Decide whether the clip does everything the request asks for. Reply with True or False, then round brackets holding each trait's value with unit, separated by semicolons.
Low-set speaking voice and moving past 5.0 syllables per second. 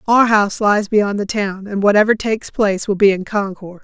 False (205 Hz; 5.5 syllables/s)